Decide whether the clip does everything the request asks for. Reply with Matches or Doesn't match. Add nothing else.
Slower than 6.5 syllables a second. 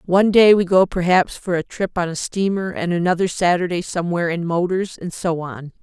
Matches